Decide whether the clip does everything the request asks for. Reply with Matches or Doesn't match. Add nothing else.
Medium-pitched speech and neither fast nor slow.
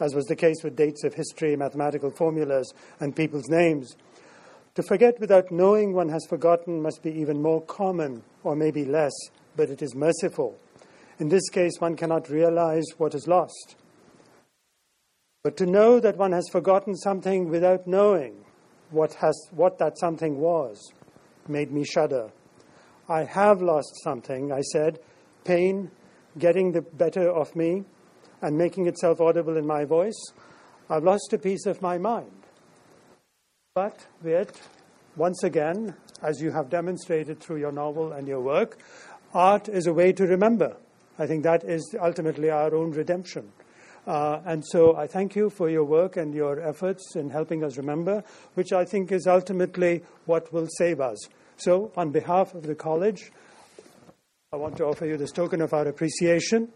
Matches